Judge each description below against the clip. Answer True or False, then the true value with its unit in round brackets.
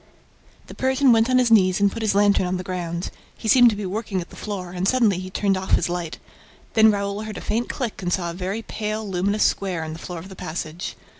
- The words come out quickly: True (250 wpm)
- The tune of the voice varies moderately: True (3.2 semitones)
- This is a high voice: True (200 Hz)